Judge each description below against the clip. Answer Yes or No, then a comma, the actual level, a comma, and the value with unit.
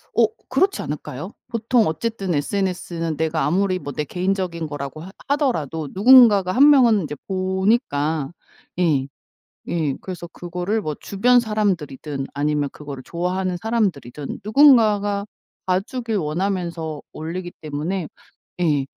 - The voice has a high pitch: No, medium, 180 Hz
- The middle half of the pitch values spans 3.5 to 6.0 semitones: Yes, average, 5.3 semitones